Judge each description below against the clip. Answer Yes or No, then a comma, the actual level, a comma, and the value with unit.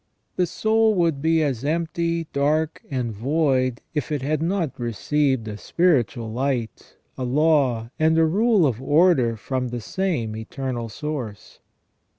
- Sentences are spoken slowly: No, average, 145 wpm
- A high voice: No, medium, 140 Hz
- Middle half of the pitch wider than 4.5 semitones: Yes, average, 5.1 semitones